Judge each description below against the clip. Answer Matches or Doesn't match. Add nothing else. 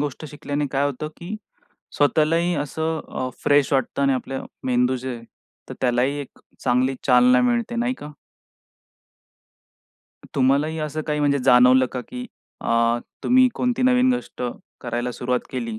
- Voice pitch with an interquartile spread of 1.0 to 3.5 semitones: Doesn't match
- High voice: Doesn't match